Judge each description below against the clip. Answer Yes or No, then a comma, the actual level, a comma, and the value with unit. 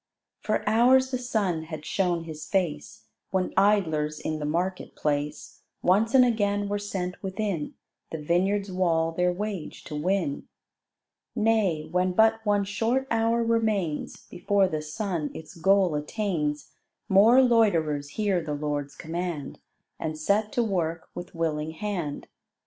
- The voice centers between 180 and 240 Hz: Yes, medium, 185 Hz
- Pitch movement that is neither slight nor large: Yes, average, 4.9 semitones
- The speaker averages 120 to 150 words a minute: Yes, average, 140 wpm